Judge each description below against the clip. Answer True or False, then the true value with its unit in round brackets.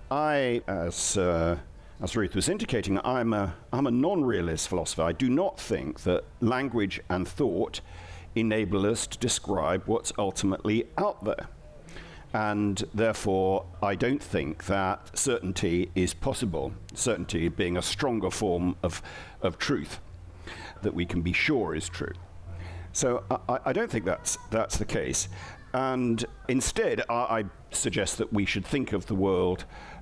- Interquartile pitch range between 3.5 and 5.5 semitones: True (3.9 semitones)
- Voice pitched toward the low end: True (95 Hz)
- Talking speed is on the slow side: False (150 wpm)